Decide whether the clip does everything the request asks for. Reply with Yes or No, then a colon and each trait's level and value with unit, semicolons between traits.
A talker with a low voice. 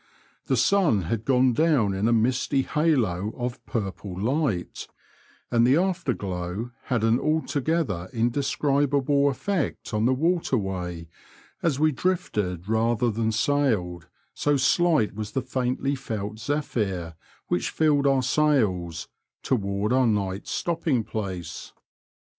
Yes: low, 120 Hz